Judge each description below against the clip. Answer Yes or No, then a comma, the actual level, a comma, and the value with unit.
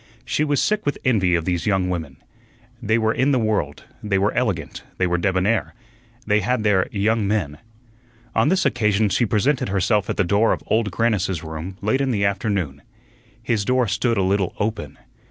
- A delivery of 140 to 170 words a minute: No, average, 190 wpm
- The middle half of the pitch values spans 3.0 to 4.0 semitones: Yes, average, 3.7 semitones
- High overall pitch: No, low, 105 Hz